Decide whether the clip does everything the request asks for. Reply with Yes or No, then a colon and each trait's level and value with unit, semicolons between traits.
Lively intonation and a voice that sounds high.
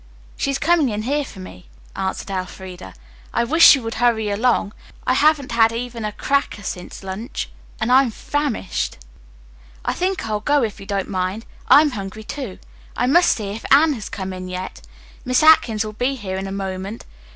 Yes: wide, 5.8 semitones; high, 220 Hz